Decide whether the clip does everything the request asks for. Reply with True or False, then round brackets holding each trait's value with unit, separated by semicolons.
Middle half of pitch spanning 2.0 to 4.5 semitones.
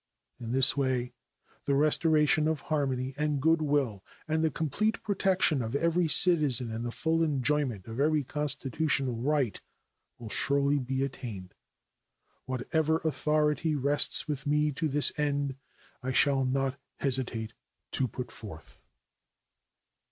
True (3.0 semitones)